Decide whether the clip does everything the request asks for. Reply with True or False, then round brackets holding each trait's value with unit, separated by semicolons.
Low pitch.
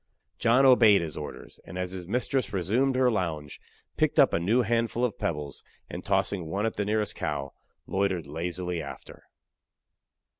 True (100 Hz)